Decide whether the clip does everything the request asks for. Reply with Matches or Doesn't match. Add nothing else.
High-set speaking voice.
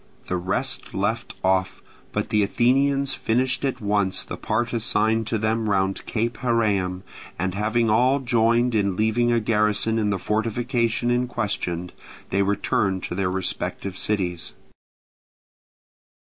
Doesn't match